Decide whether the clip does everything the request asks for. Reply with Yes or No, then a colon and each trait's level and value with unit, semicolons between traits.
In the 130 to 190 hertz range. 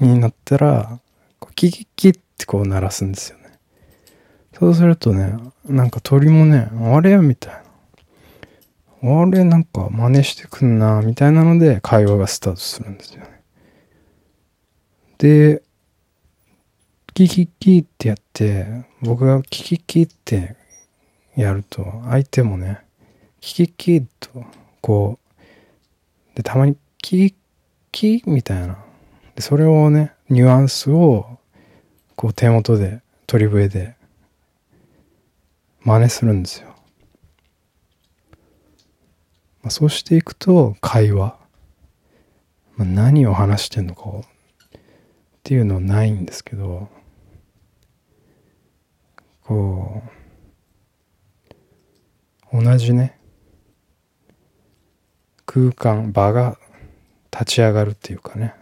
No: low, 115 Hz